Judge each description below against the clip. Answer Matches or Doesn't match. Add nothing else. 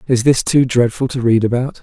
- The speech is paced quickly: Matches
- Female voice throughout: Doesn't match